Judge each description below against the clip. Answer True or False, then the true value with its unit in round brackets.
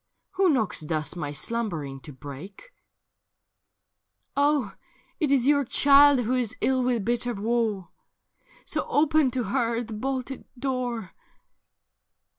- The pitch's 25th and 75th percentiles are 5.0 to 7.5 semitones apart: True (5.3 semitones)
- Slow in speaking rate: True (130 wpm)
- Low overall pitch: False (240 Hz)